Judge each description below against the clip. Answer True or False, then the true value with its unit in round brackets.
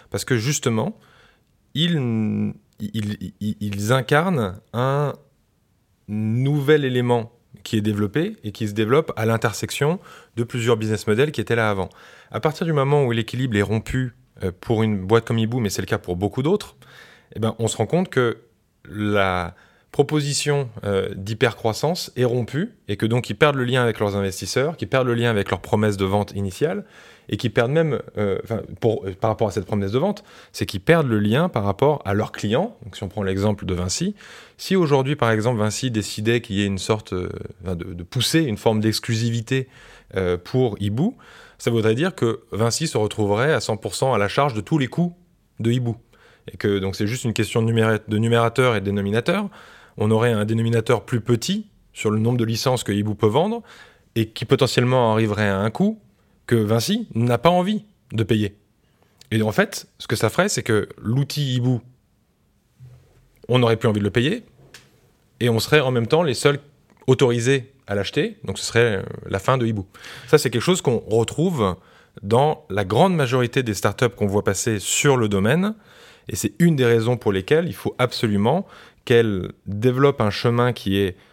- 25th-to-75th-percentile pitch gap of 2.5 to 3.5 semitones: False (4.3 semitones)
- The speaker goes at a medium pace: True (190 wpm)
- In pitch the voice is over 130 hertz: False (115 Hz)